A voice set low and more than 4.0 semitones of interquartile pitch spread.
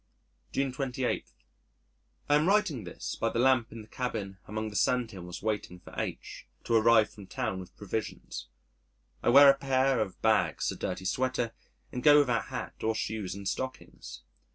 Yes: low, 115 Hz; average, 4.6 semitones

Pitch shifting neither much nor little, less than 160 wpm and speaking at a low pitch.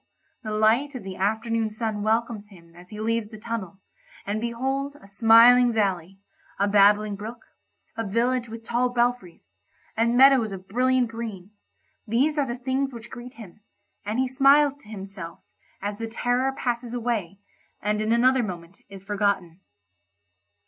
No: average, 3.3 semitones; average, 150 wpm; high, 225 Hz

